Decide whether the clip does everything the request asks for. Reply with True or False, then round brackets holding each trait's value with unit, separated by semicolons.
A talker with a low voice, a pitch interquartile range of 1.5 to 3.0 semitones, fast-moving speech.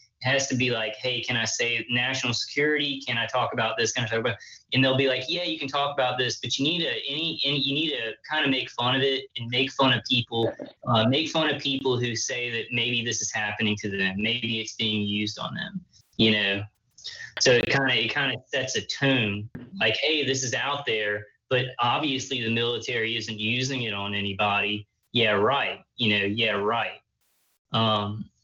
False (120 Hz; 3.5 semitones; 215 wpm)